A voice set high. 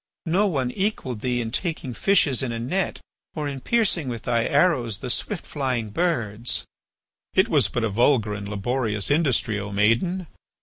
No: low, 125 Hz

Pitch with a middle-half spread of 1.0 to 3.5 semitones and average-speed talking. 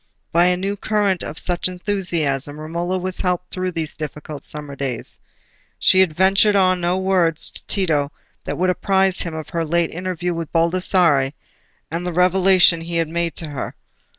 Yes: narrow, 2.6 semitones; average, 175 wpm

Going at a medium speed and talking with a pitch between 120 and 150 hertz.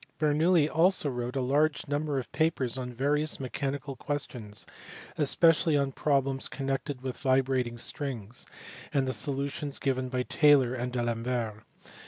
Yes: average, 150 wpm; low, 135 Hz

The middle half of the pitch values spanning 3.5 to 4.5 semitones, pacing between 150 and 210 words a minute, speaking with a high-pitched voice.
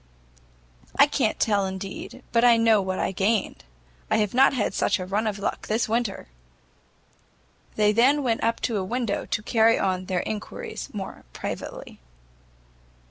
No: average, 3.1 semitones; average, 160 wpm; high, 215 Hz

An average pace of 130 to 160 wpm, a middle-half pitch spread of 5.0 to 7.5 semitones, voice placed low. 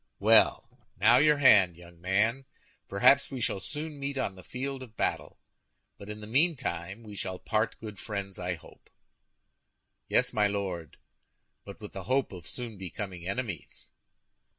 Yes: average, 155 wpm; average, 5.3 semitones; low, 105 Hz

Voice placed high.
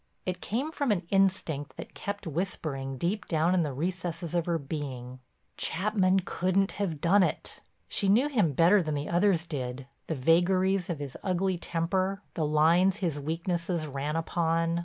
No: medium, 170 Hz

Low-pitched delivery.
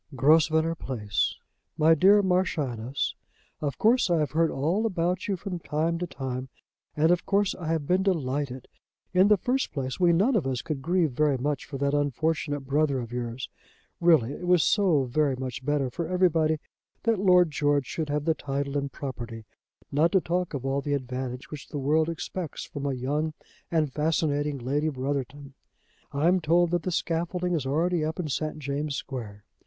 No: medium, 150 Hz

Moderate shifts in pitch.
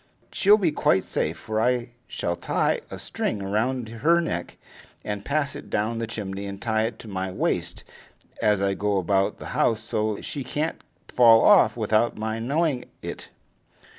Yes: average, 3.7 semitones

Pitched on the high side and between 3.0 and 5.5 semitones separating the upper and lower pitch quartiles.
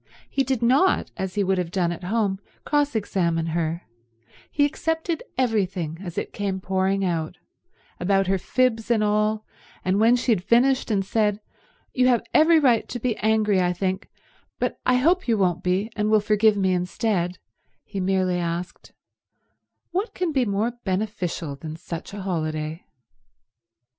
Yes: high, 200 Hz; average, 4.5 semitones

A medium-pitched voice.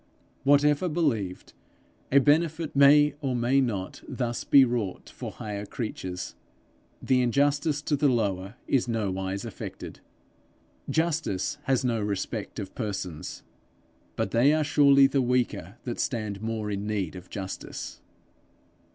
No: low, 120 Hz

